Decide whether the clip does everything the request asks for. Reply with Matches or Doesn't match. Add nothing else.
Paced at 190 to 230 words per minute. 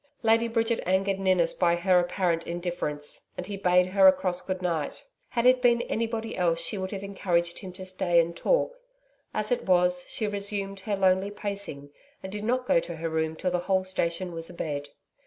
Matches